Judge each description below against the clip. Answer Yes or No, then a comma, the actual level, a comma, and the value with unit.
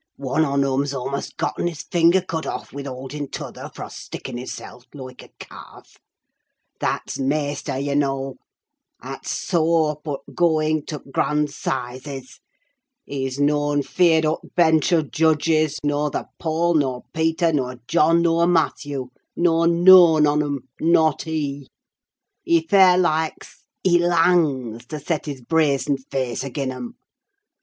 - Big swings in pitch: No, average, 3.0 semitones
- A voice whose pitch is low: No, medium, 150 Hz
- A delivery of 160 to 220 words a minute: No, average, 145 wpm